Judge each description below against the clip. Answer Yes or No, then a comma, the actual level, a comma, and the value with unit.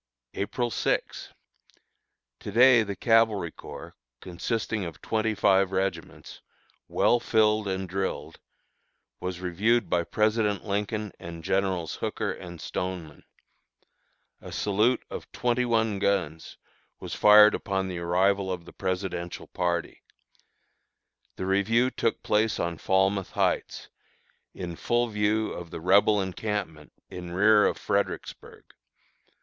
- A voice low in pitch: Yes, low, 100 Hz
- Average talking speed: No, slow, 120 wpm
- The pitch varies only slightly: No, average, 3.2 semitones